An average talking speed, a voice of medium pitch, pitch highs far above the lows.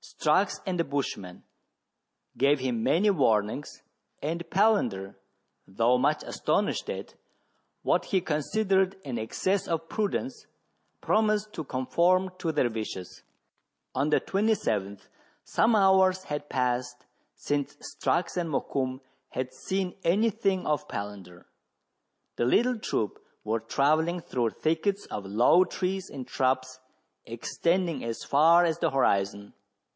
No: slow, 125 wpm; medium, 150 Hz; wide, 7.2 semitones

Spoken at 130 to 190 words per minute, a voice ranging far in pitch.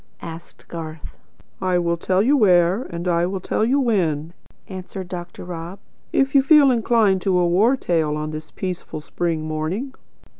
No: average, 165 wpm; average, 4.2 semitones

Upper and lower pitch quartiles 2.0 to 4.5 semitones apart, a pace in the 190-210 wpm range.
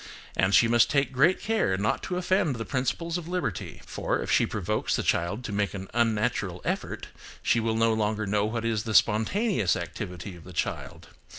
No: average, 5.2 semitones; average, 195 wpm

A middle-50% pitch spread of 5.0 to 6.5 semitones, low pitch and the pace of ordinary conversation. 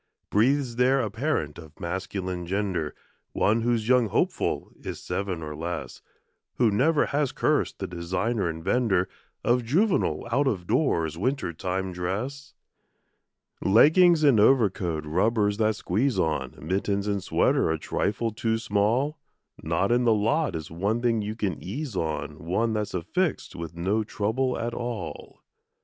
Yes: wide, 5.5 semitones; low, 105 Hz; average, 150 wpm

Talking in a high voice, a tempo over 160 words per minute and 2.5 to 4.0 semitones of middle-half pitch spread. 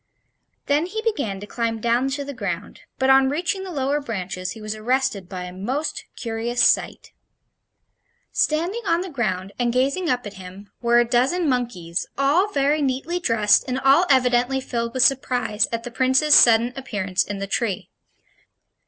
No: very high, 250 Hz; average, 170 wpm; average, 4.4 semitones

